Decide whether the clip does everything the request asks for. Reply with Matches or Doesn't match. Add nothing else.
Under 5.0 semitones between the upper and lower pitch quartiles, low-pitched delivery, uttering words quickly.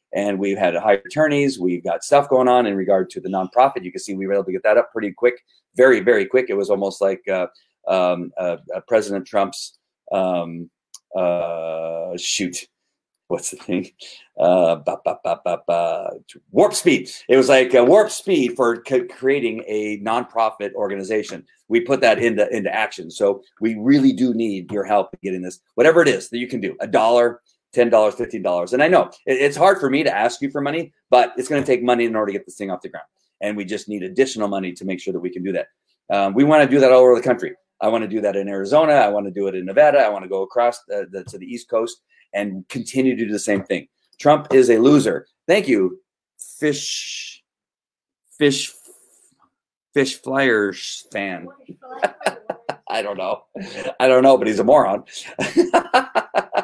Doesn't match